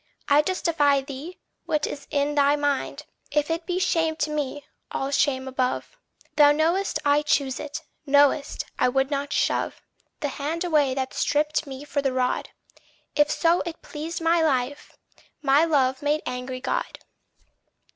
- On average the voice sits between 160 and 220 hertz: No, very high, 290 Hz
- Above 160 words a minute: No, average, 155 wpm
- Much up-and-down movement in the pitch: No, narrow, 2.4 semitones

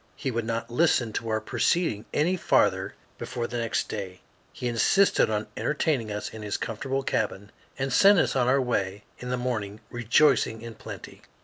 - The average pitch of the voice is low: Yes, low, 120 Hz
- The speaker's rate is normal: Yes, average, 180 wpm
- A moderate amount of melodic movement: Yes, average, 3.6 semitones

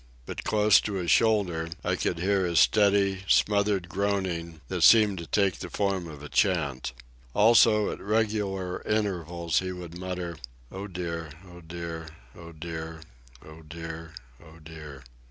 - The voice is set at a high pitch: No, very low, 90 Hz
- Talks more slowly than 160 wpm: Yes, average, 150 wpm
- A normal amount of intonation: Yes, average, 3.4 semitones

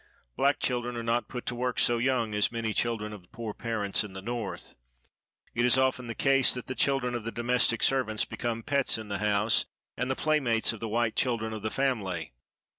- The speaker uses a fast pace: Yes, fast, 210 wpm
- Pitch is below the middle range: Yes, low, 115 Hz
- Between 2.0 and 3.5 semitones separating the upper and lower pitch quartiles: Yes, narrow, 2.4 semitones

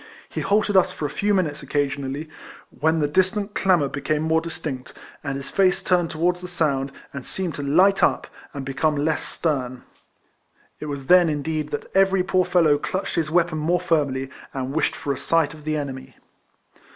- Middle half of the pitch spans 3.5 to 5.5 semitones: Yes, average, 4.0 semitones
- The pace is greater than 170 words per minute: Yes, average, 190 wpm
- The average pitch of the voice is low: No, medium, 155 Hz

